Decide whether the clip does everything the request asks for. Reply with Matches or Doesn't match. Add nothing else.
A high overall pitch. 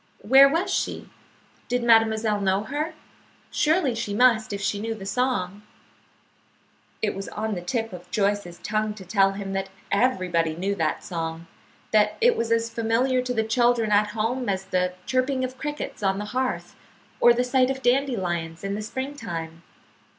Matches